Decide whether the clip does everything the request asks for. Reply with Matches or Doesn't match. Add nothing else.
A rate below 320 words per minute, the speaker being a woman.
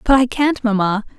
Matches